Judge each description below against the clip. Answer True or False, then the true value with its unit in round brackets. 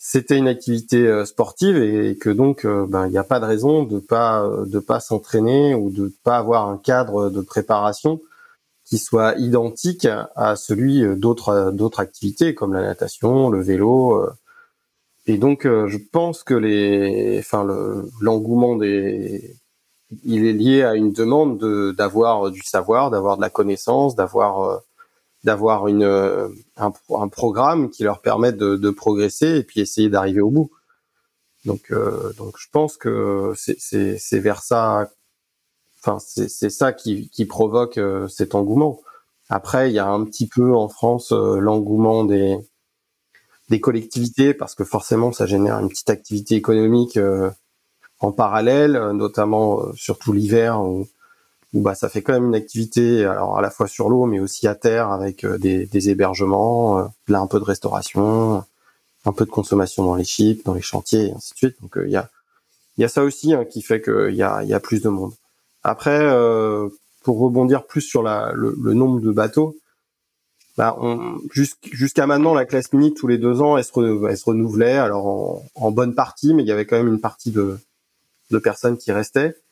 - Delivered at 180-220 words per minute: True (185 wpm)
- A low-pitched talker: True (110 Hz)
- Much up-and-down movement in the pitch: False (4.0 semitones)